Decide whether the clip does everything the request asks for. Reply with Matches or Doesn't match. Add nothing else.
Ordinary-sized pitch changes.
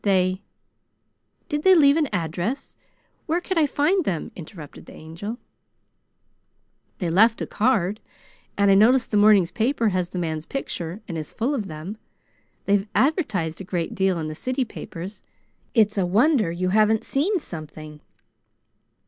Doesn't match